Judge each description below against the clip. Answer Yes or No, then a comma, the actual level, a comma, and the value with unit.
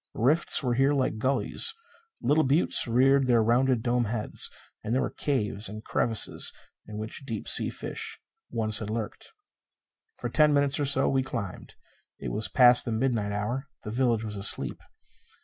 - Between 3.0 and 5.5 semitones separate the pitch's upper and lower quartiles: Yes, average, 3.7 semitones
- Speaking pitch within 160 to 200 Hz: No, low, 120 Hz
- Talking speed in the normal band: Yes, average, 165 wpm